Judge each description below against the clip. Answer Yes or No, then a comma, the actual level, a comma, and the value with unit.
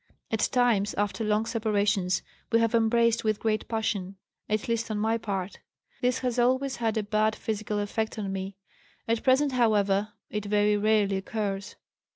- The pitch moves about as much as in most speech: No, narrow, 2.0 semitones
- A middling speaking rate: Yes, average, 165 wpm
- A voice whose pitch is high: Yes, high, 215 Hz